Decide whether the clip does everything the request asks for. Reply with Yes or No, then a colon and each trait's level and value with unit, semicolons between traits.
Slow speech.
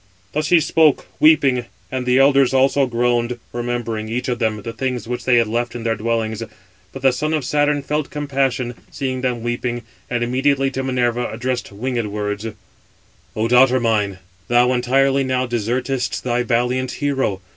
No: average, 165 wpm